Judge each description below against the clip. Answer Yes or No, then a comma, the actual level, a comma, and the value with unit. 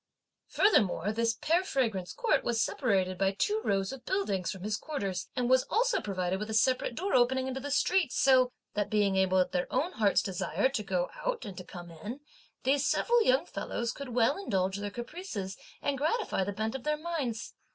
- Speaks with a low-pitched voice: No, high, 235 Hz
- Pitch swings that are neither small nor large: No, wide, 6.6 semitones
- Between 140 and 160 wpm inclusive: No, average, 200 wpm